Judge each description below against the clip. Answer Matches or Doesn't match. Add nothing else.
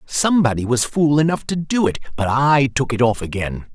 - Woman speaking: Doesn't match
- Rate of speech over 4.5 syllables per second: Matches